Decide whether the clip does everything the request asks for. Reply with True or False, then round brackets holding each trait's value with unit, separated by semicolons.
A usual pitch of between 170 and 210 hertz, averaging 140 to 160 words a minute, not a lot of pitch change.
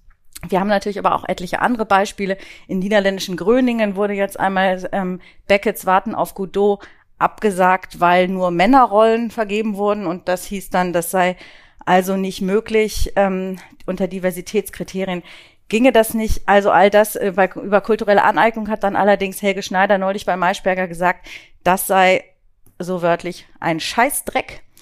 True (190 Hz; 150 wpm; 2.1 semitones)